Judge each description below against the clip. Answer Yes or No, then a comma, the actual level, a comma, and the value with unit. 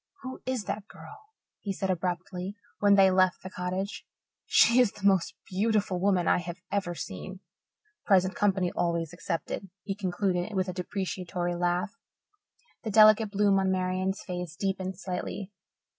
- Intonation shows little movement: Yes, narrow, 2.1 semitones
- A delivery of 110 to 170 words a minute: Yes, average, 155 wpm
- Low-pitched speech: No, high, 190 Hz